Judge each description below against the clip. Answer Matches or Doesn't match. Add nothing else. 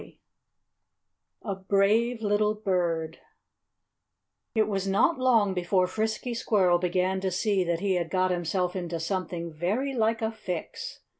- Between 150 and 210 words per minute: Doesn't match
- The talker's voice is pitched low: Doesn't match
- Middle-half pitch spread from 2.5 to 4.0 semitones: Matches